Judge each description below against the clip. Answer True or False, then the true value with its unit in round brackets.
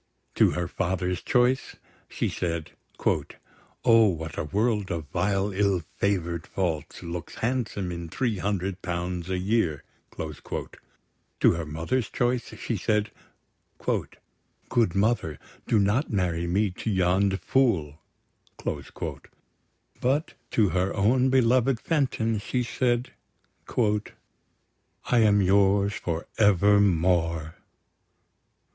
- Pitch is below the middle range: True (100 Hz)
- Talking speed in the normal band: False (105 wpm)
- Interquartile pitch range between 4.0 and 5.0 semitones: True (4.6 semitones)